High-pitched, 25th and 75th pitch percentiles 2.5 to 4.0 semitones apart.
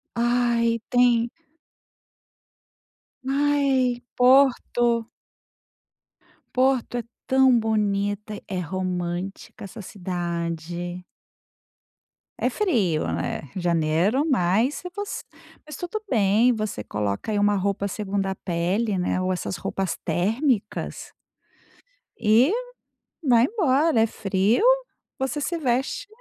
No: high, 220 Hz; wide, 5.5 semitones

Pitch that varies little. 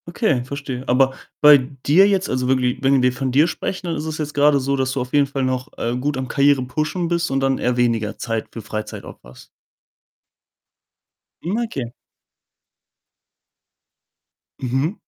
No: average, 3.0 semitones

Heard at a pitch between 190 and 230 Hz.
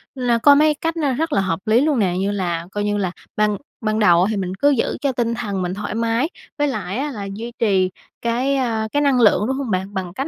Yes: high, 220 Hz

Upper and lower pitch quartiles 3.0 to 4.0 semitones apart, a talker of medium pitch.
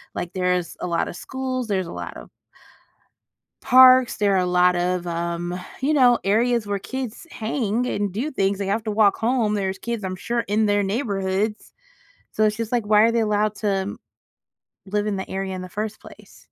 No: average, 3.4 semitones; high, 205 Hz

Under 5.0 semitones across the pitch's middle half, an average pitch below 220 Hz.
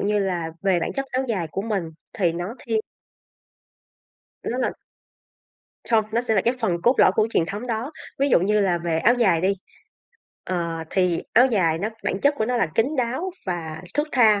No: average, 5.3 semitones; high, 210 Hz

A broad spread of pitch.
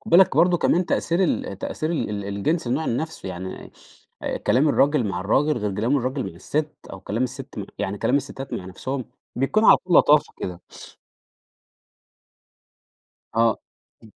Yes: wide, 6.8 semitones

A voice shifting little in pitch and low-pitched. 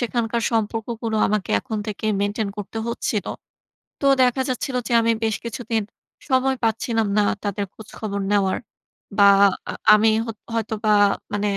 No: narrow, 1.9 semitones; high, 220 Hz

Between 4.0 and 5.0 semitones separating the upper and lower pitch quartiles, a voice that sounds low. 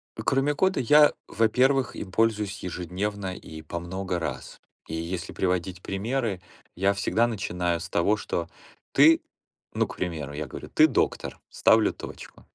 Yes: average, 4.6 semitones; very low, 95 Hz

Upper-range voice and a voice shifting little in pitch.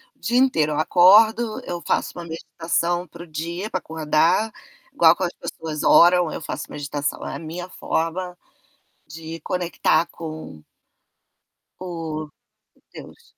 No: medium, 170 Hz; narrow, 2.3 semitones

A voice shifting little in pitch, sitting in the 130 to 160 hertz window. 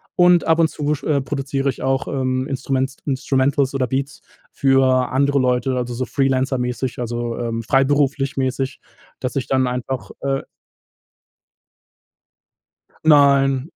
Yes: narrow, 1.4 semitones; low, 135 Hz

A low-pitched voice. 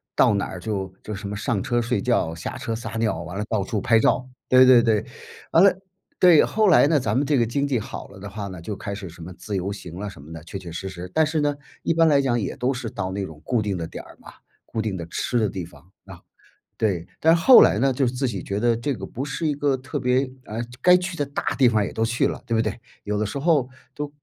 Yes: low, 115 Hz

